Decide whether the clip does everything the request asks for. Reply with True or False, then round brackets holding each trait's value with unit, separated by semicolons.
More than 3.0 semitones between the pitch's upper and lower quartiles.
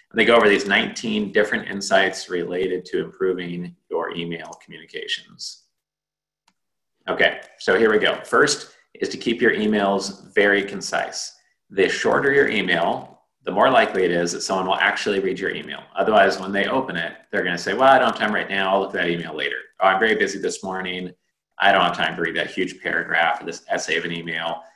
True (3.7 semitones)